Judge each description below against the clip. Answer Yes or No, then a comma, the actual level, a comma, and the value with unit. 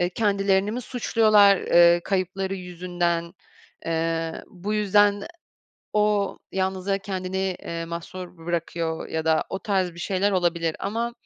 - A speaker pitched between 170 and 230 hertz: Yes, medium, 185 Hz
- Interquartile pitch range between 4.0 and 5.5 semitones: No, average, 2.8 semitones